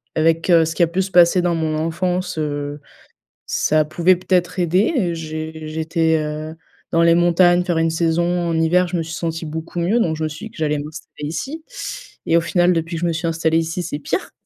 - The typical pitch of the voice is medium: Yes, medium, 165 Hz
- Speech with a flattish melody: Yes, narrow, 1.8 semitones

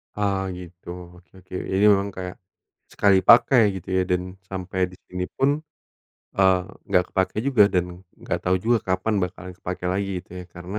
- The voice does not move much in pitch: Yes, narrow, 1.8 semitones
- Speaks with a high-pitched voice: No, very low, 95 Hz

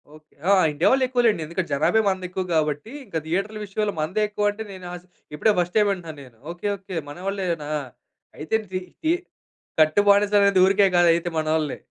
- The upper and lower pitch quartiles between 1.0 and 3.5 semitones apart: No, average, 4.4 semitones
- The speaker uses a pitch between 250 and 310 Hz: No, medium, 185 Hz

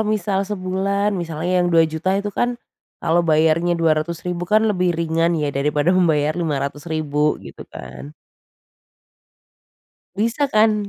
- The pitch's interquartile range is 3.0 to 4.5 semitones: Yes, average, 4.2 semitones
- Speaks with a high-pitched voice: No, medium, 170 Hz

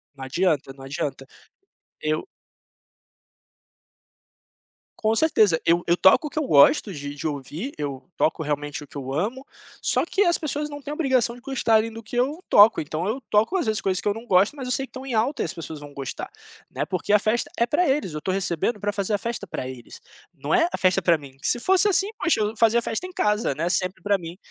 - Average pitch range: No, wide, 8.2 semitones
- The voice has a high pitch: Yes, high, 205 Hz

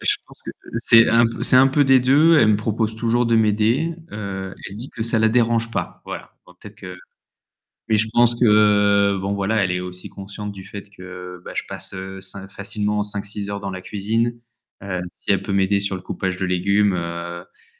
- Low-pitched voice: Yes, low, 105 Hz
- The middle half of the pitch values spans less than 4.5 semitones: Yes, average, 3.1 semitones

